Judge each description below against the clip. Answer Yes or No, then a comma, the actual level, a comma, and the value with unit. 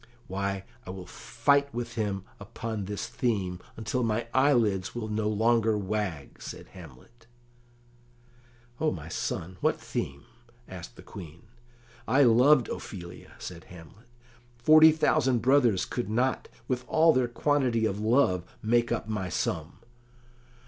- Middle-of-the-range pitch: No, low, 110 Hz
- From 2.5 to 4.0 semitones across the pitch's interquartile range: No, average, 4.6 semitones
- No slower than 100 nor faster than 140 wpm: Yes, slow, 135 wpm